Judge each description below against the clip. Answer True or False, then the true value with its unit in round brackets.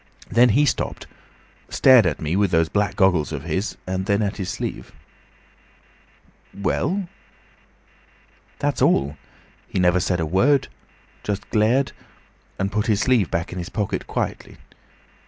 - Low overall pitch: True (100 Hz)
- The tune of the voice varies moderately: True (3.8 semitones)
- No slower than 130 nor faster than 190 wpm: True (140 wpm)